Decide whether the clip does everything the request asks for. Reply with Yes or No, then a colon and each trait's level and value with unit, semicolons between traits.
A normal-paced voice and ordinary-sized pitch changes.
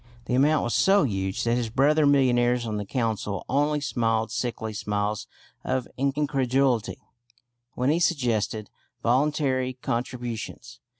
No: slow, 125 wpm; average, 3.5 semitones